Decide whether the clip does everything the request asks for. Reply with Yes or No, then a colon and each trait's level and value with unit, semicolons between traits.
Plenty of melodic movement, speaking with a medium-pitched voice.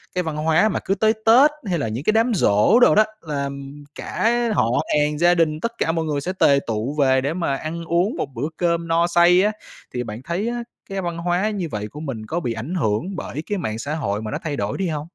No: average, 4.8 semitones; medium, 165 Hz